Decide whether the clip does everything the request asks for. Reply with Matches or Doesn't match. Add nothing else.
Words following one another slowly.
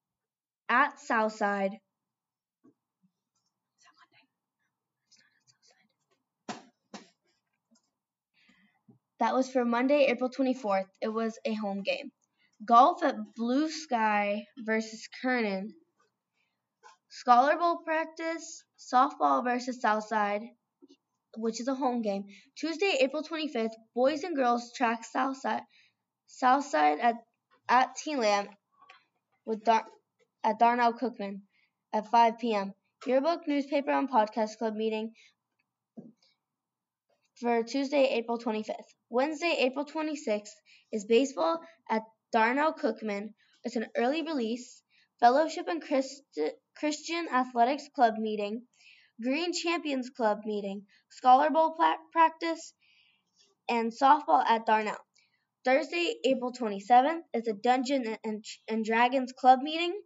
Matches